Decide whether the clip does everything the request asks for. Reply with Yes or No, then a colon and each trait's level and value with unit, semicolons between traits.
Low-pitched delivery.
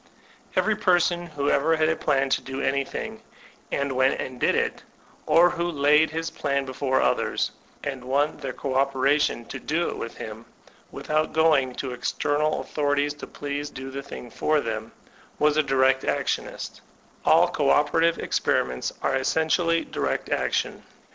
No: medium, 145 Hz